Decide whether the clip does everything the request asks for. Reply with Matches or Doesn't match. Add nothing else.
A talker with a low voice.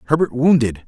Matches